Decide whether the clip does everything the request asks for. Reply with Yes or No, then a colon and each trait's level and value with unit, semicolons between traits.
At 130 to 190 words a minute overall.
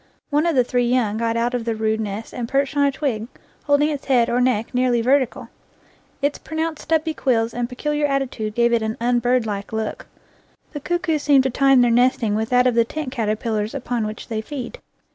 No: fast, 205 wpm